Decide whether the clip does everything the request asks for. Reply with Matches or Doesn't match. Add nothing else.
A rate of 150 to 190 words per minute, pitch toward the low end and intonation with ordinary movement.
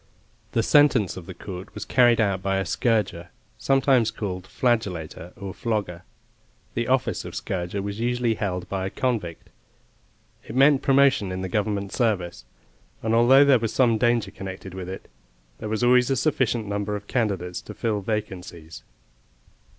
Matches